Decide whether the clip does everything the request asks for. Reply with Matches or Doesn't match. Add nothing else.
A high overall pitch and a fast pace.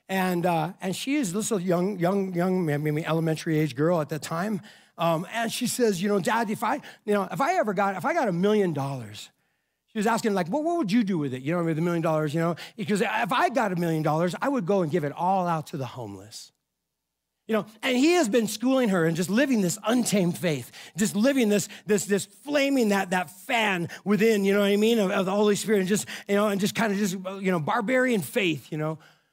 Matches